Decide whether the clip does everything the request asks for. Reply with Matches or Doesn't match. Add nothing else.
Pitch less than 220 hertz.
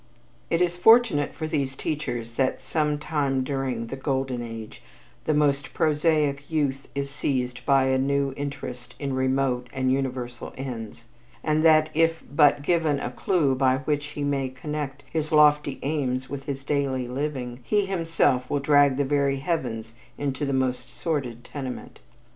Matches